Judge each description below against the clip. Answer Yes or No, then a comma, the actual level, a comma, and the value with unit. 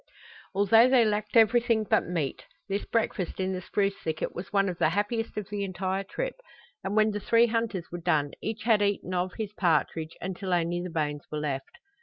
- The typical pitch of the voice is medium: No, high, 195 Hz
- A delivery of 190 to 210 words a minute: Yes, average, 200 wpm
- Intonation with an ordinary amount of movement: Yes, average, 3.7 semitones